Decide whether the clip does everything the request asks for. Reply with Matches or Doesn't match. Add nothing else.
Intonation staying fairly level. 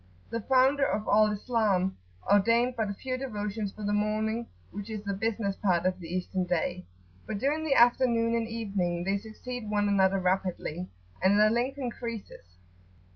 Doesn't match